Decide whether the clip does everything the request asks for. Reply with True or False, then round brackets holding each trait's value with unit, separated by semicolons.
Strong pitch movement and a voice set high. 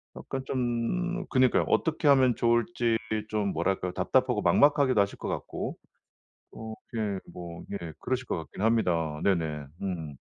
False (6.4 semitones; 110 Hz)